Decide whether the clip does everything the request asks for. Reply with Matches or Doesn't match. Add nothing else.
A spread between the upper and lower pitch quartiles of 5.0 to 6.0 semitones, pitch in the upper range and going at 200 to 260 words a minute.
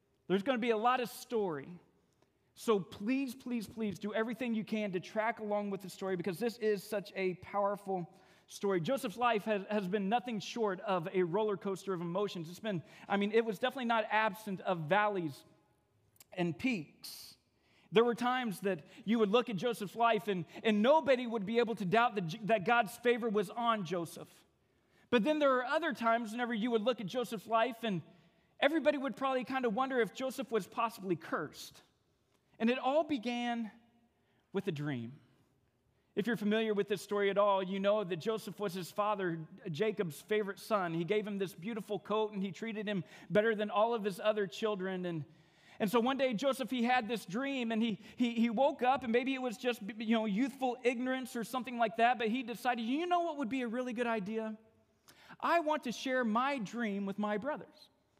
Doesn't match